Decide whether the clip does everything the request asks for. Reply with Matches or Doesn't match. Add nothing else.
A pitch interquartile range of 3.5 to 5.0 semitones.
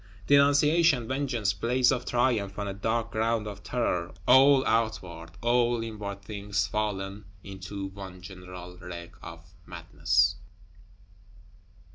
Matches